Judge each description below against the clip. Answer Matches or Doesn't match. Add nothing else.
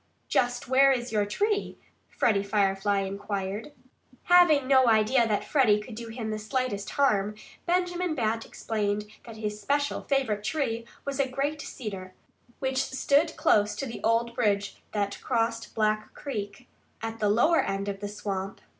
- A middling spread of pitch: Matches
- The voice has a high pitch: Matches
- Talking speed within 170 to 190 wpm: Doesn't match